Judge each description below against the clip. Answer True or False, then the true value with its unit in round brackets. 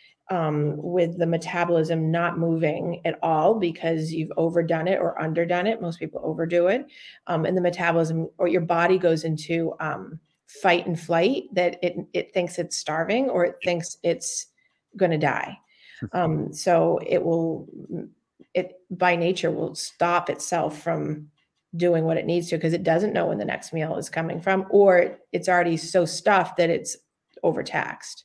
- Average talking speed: True (170 wpm)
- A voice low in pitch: False (170 Hz)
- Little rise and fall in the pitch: True (1.5 semitones)